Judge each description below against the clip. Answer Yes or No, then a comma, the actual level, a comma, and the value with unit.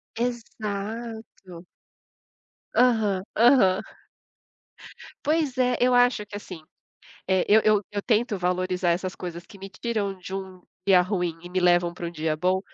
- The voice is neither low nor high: No, high, 195 Hz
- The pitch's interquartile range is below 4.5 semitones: Yes, average, 3.8 semitones